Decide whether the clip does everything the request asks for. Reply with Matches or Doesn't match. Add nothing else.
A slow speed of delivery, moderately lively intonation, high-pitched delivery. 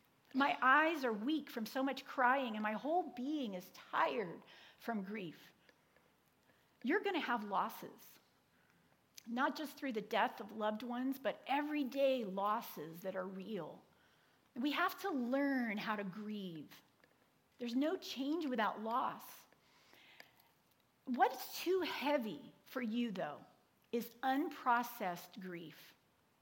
Matches